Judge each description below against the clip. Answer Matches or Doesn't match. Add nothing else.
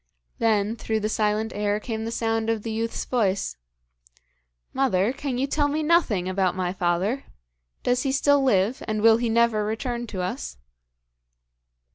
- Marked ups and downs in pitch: Doesn't match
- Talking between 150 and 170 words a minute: Matches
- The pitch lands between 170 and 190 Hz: Doesn't match